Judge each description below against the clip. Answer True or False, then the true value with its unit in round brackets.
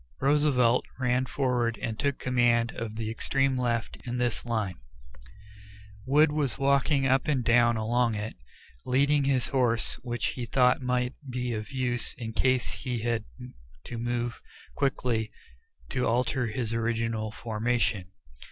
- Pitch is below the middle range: True (120 Hz)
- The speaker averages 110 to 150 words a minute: True (140 wpm)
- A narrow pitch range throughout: True (2.1 semitones)